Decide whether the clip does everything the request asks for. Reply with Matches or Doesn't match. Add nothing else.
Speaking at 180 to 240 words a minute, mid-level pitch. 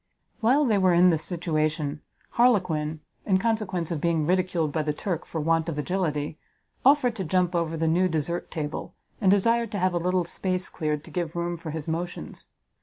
Matches